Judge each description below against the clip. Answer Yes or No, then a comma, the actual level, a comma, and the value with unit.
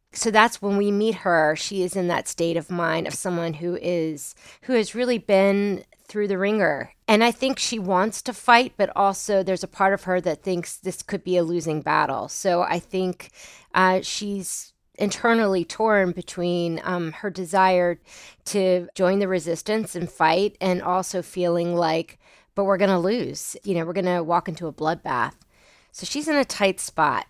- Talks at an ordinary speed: Yes, average, 185 wpm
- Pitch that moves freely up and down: No, narrow, 2.6 semitones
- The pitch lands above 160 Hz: Yes, medium, 185 Hz